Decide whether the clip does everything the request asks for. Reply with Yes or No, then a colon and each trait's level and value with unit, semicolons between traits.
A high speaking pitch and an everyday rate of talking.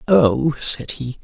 No: low, 135 Hz; average, 145 wpm